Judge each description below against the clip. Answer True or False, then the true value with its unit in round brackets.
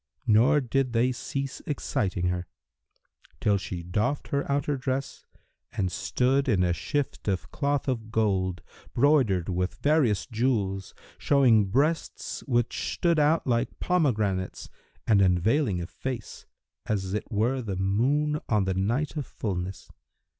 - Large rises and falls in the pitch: True (6.3 semitones)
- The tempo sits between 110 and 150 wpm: True (135 wpm)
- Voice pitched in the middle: False (115 Hz)